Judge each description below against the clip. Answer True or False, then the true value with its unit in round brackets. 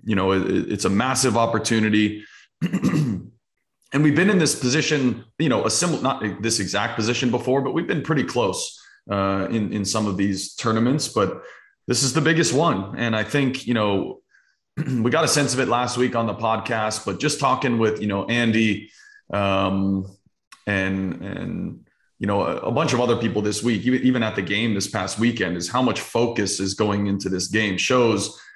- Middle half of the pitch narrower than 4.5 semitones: True (4.0 semitones)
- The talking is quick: False (195 wpm)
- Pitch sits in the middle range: False (115 Hz)